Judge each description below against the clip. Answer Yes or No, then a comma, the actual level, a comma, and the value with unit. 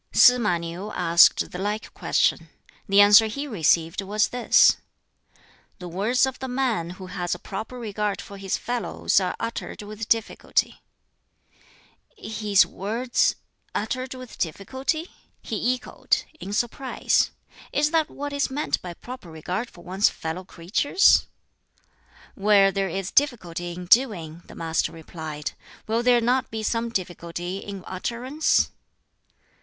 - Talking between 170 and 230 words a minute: No, average, 140 wpm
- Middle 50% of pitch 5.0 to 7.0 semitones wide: Yes, wide, 5.4 semitones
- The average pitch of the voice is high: Yes, high, 210 Hz